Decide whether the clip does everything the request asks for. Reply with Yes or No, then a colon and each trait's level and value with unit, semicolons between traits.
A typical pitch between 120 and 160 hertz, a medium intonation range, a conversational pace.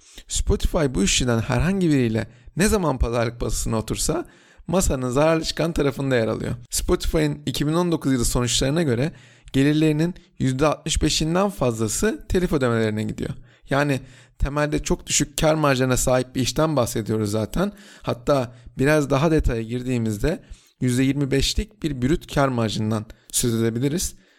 Yes: low, 135 Hz; average, 4.2 semitones; average, 125 wpm